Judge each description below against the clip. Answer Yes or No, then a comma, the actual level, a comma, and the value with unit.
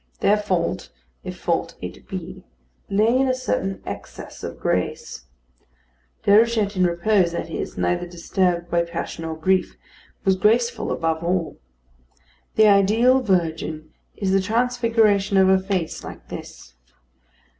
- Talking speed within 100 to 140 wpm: Yes, slow, 135 wpm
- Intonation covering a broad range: No, average, 4.1 semitones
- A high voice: Yes, high, 195 Hz